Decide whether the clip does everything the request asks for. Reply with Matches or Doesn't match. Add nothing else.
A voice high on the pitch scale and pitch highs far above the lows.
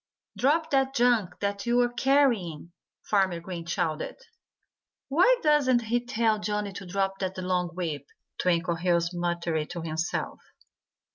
Matches